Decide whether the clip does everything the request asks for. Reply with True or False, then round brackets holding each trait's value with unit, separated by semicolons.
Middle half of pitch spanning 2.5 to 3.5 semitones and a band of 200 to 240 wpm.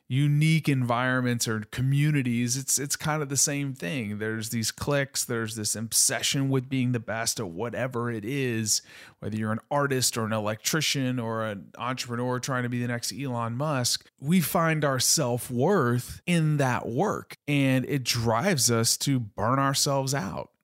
False (3.2 semitones; 165 wpm)